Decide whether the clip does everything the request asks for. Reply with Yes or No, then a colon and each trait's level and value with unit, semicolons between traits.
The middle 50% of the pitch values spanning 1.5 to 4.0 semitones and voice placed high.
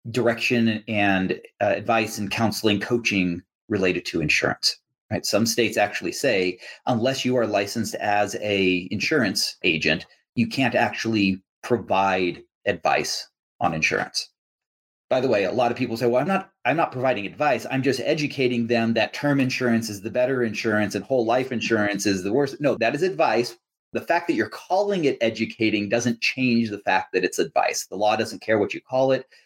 No: average, 3.4 semitones; low, 115 Hz